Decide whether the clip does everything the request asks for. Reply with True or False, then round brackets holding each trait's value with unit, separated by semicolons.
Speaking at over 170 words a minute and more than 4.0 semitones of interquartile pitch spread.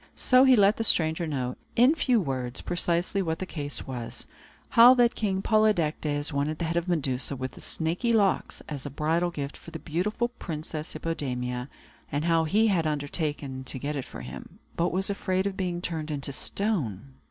True (190 wpm; 5.3 semitones)